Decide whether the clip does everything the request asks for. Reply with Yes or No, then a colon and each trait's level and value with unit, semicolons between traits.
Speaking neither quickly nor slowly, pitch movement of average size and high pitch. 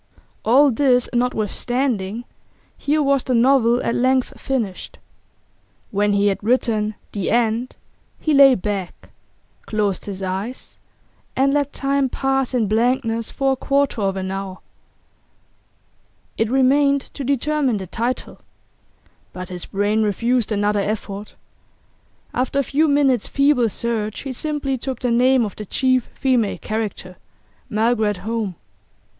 No: slow, 130 wpm; average, 4.3 semitones; high, 235 Hz